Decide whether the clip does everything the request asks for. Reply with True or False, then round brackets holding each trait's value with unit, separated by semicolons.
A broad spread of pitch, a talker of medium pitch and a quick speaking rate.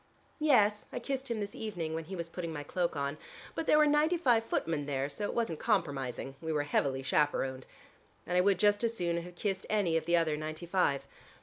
True (5.8 semitones; 175 Hz; 220 wpm)